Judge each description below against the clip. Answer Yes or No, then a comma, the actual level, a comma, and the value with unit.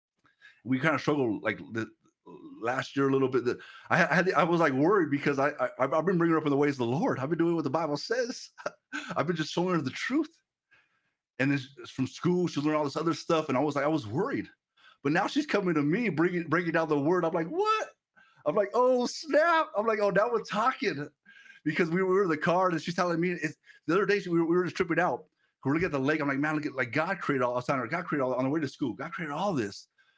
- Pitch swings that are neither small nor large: Yes, average, 4.6 semitones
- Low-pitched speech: No, medium, 165 Hz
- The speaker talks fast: Yes, fast, 270 wpm